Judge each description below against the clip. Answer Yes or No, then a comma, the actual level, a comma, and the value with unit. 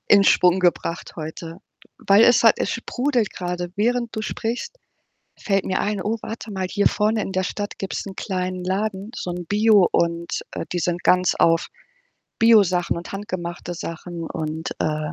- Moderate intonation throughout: Yes, average, 3.4 semitones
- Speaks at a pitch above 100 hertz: Yes, medium, 185 Hz